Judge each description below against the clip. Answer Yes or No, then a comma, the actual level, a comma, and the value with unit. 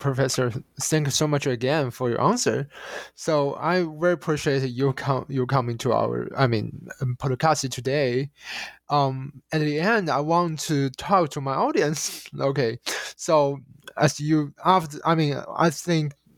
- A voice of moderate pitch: Yes, medium, 145 Hz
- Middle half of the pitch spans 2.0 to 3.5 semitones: Yes, average, 2.7 semitones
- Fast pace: No, average, 160 wpm